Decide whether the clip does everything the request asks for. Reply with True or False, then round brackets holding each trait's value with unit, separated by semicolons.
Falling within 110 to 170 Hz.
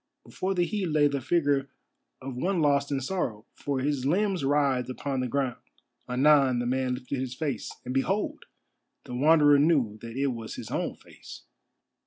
True (140 Hz)